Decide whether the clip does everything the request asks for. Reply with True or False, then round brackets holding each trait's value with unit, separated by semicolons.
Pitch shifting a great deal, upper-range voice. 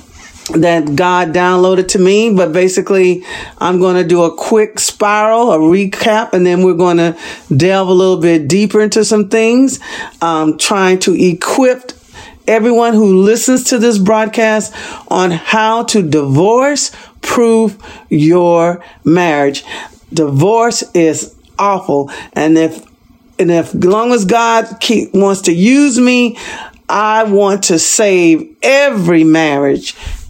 False (4.6 semitones; 195 Hz)